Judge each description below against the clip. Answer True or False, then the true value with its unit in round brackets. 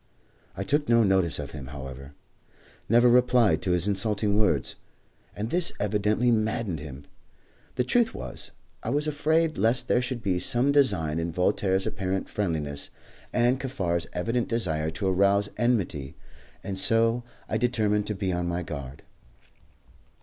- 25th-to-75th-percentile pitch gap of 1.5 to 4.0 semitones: False (5.6 semitones)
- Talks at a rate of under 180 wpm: True (150 wpm)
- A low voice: True (105 Hz)